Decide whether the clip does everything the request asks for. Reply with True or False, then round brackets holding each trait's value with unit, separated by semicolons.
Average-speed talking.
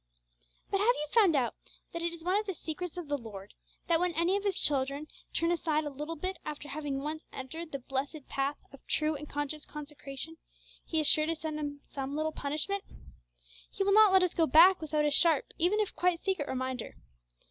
False (215 wpm)